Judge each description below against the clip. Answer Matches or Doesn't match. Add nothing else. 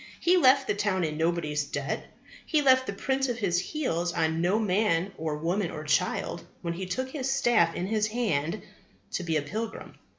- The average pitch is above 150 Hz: Matches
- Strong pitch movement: Matches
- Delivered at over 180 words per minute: Matches